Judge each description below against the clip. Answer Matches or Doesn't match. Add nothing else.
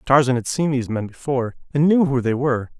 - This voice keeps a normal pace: Doesn't match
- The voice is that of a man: Matches